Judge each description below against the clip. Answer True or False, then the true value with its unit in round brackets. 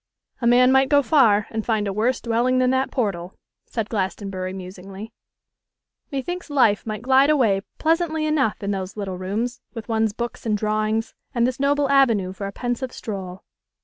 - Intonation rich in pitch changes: False (4.6 semitones)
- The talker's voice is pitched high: True (225 Hz)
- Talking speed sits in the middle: True (180 wpm)